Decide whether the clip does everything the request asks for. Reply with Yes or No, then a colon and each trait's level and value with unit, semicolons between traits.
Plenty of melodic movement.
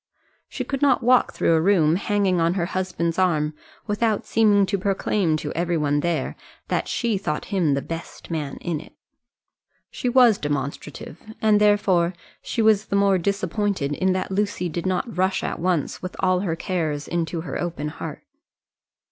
No: average, 3.8 semitones